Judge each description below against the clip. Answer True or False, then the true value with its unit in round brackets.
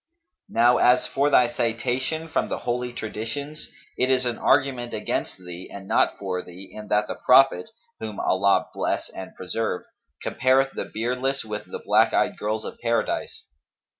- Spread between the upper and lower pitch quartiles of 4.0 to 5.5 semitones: False (3.6 semitones)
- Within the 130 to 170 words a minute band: True (165 wpm)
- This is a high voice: False (120 Hz)